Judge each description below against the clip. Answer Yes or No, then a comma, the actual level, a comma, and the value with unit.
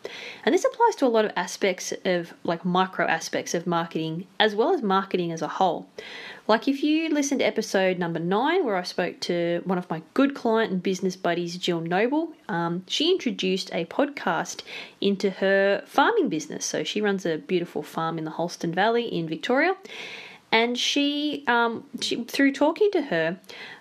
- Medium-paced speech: Yes, average, 180 wpm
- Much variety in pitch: Yes, wide, 6.2 semitones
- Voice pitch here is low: No, high, 195 Hz